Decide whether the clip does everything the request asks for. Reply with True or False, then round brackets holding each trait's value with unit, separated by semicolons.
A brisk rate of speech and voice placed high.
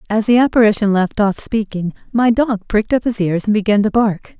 True (220 wpm; 215 Hz)